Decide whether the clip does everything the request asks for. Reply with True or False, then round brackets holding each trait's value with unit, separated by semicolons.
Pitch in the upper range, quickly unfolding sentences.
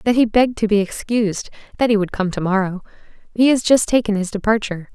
True (215 Hz; 220 wpm)